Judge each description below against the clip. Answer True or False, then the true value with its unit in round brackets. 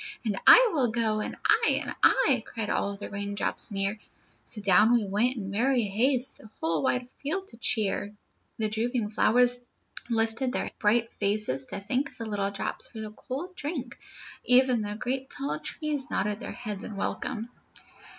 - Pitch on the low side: False (225 Hz)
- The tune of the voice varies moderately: True (3.5 semitones)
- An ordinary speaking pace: True (170 wpm)